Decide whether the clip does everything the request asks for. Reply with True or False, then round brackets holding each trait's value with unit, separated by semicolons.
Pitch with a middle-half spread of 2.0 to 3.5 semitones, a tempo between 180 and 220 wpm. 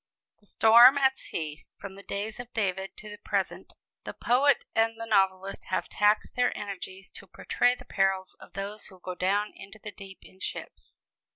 True (2.7 semitones; 185 wpm)